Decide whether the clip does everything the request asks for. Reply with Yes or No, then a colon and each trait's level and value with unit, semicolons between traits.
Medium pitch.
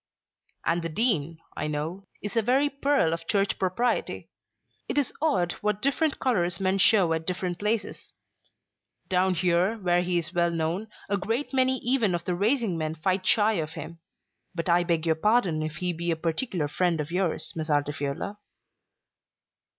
Yes: medium, 180 Hz